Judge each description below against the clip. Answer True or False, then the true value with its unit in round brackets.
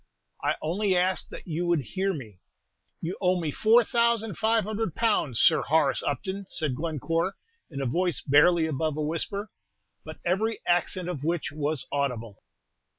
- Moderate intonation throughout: True (4.8 semitones)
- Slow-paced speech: False (165 wpm)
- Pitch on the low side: False (170 Hz)